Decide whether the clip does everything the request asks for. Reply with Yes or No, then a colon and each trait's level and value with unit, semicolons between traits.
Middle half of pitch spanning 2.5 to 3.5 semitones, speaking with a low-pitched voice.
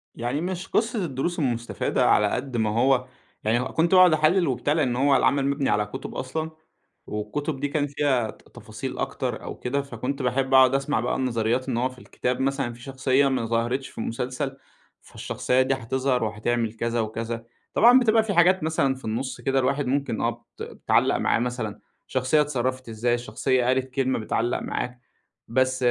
Yes: average, 2.8 semitones; low, 130 Hz